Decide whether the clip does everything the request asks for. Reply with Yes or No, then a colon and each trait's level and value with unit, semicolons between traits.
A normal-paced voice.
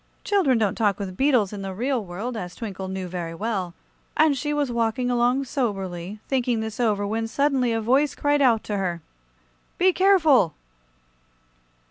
Yes: average, 165 wpm